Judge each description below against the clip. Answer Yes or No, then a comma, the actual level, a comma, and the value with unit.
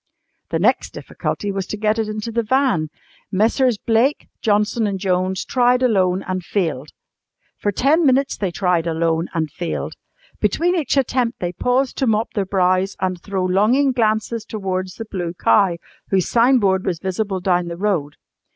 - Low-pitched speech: No, high, 200 Hz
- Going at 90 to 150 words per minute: No, average, 165 wpm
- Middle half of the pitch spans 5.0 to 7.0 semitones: No, average, 4.2 semitones